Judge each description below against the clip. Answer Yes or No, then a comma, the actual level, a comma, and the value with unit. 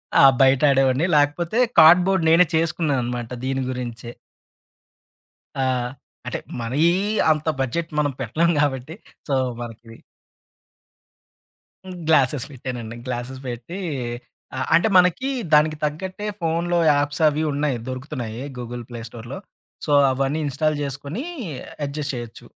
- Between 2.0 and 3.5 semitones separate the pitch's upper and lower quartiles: No, average, 4.2 semitones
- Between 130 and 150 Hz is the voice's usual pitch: Yes, medium, 140 Hz